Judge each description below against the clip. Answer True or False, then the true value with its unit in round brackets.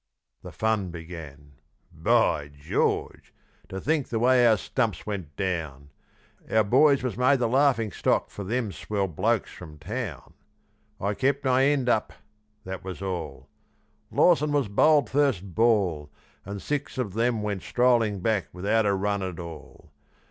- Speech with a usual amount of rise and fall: False (5.7 semitones)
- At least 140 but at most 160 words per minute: True (150 wpm)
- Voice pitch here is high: False (105 Hz)